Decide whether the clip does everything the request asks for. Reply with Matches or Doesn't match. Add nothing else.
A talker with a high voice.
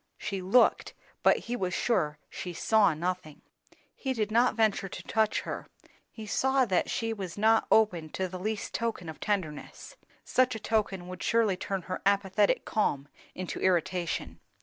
Matches